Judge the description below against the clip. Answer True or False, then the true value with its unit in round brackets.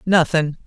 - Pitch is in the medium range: True (160 Hz)